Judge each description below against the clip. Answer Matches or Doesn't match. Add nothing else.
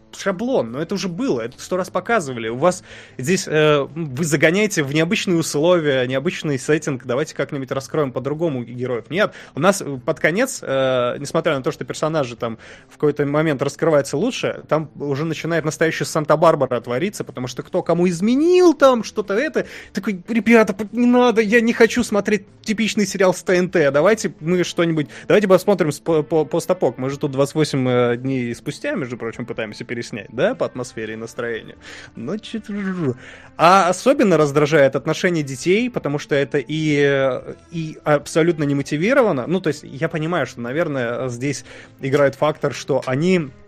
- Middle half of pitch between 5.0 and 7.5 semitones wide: Matches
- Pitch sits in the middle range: Matches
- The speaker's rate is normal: Doesn't match